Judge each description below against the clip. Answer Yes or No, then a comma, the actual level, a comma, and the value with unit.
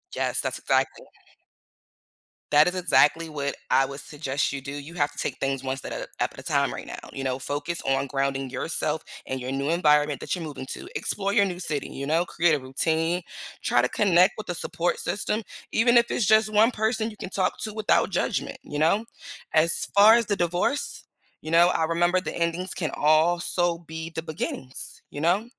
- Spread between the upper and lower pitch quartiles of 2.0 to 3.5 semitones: No, average, 4.2 semitones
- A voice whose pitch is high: No, medium, 165 Hz